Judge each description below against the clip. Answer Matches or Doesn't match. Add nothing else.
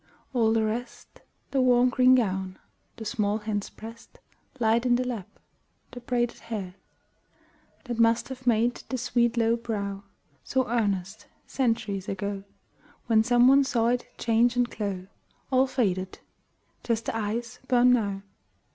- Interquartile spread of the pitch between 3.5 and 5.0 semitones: Doesn't match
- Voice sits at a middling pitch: Doesn't match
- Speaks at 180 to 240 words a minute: Doesn't match